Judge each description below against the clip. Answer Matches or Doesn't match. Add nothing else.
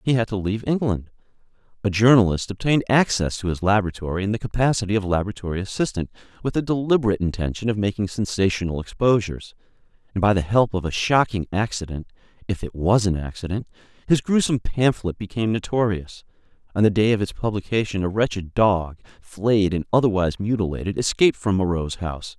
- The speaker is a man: Matches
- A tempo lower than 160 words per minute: Doesn't match